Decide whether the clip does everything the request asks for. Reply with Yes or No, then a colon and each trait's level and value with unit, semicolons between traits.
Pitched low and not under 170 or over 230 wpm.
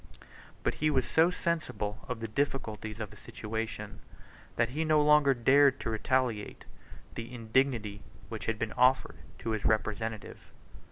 No: low, 115 Hz; average, 150 wpm